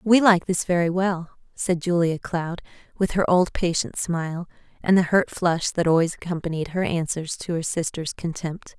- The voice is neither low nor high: Yes, medium, 175 Hz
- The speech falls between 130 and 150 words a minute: No, average, 180 wpm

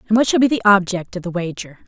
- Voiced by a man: No, female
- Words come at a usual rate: No, fast, 290 wpm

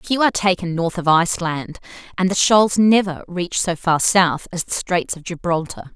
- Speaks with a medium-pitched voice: Yes, medium, 180 Hz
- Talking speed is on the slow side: No, average, 190 wpm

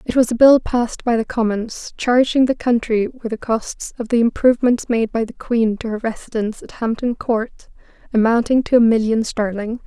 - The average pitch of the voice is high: Yes, high, 230 Hz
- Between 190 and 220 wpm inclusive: Yes, average, 195 wpm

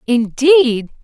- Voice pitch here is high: Yes, very high, 265 Hz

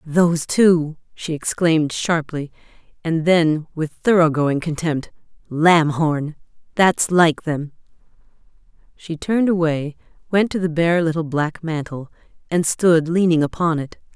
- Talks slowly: Yes, slow, 125 wpm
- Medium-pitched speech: Yes, medium, 160 Hz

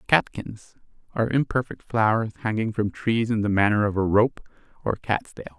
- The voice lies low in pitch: Yes, low, 110 Hz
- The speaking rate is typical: Yes, average, 170 wpm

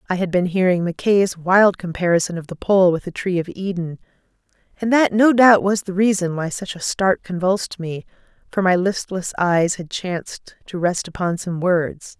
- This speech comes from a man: No, female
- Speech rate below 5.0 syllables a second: Yes, 4.8 syllables/s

